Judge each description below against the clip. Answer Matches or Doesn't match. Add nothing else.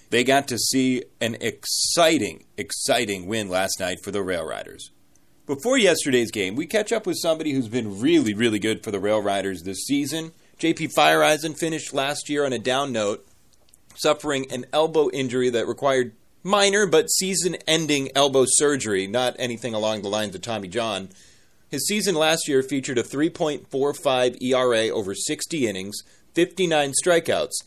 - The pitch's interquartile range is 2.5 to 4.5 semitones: Doesn't match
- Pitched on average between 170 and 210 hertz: Doesn't match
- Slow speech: Doesn't match